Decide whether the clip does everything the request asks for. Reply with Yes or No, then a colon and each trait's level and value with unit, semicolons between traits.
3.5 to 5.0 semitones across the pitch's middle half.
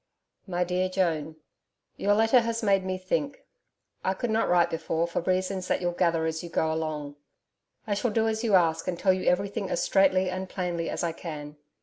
No: average, 2.9 semitones